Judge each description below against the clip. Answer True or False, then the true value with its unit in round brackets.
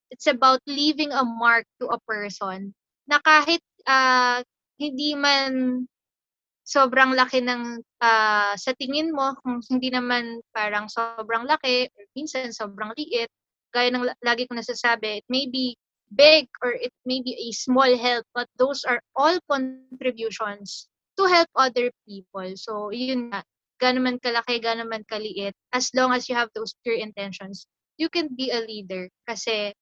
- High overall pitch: True (245 Hz)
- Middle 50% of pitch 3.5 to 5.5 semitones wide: False (2.8 semitones)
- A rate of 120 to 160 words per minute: True (155 wpm)